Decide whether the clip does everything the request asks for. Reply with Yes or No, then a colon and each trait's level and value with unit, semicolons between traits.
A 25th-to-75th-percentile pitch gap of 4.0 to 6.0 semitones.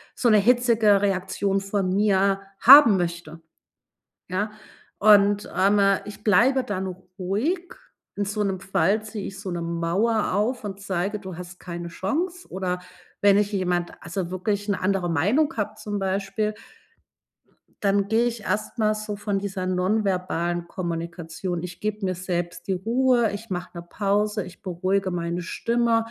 No: average, 2.8 semitones